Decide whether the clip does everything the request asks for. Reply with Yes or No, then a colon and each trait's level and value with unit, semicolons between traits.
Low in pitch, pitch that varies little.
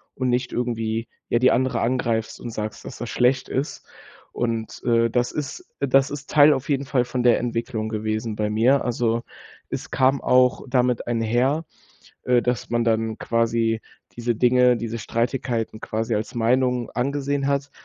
Yes: low, 120 Hz; narrow, 2.2 semitones